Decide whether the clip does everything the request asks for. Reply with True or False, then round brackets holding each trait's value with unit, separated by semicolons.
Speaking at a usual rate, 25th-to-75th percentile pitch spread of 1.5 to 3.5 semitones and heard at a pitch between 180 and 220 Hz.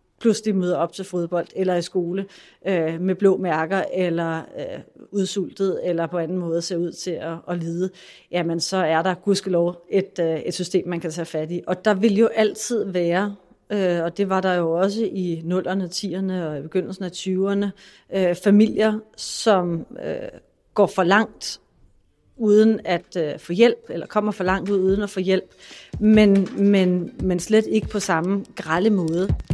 True (185 wpm; 2.6 semitones; 185 Hz)